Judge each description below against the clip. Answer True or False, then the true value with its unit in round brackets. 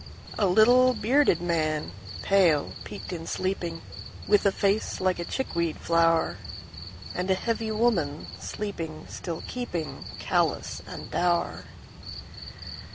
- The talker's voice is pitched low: False (180 Hz)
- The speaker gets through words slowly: True (100 wpm)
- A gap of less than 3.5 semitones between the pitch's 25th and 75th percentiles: False (4.3 semitones)